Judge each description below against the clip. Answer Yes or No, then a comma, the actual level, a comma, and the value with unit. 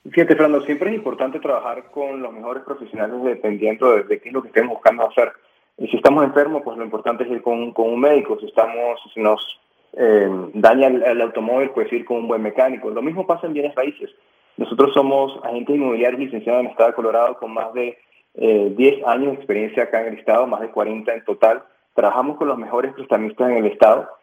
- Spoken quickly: Yes, fast, 225 wpm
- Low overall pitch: Yes, low, 120 Hz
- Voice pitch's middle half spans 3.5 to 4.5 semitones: Yes, average, 3.8 semitones